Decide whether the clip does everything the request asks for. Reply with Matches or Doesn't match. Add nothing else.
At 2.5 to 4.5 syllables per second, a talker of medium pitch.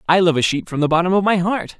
Doesn't match